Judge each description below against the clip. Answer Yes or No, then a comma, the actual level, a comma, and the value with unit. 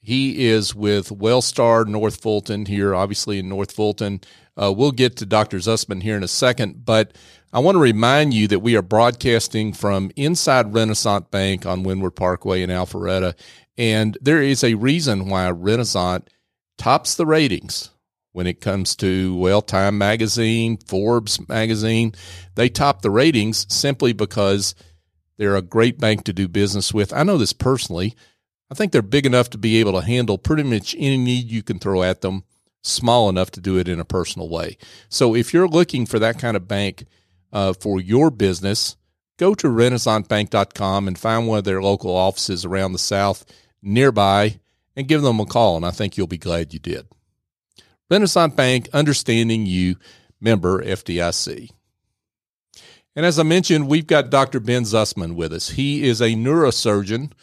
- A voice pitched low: Yes, low, 105 Hz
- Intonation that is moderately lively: Yes, average, 3.8 semitones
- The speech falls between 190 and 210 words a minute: No, average, 175 wpm